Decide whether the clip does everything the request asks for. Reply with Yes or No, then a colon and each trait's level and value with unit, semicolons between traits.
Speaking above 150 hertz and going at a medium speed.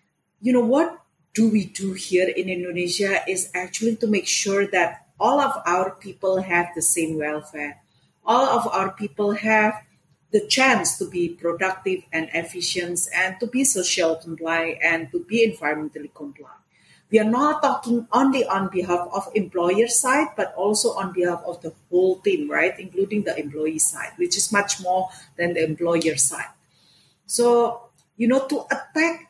Yes: high, 190 Hz; average, 165 wpm